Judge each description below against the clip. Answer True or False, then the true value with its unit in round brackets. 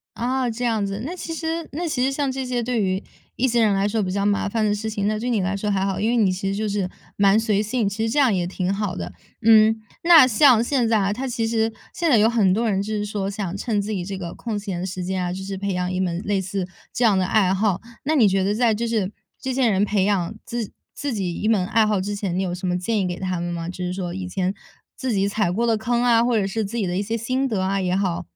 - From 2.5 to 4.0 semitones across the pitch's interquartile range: True (3.4 semitones)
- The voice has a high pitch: True (210 Hz)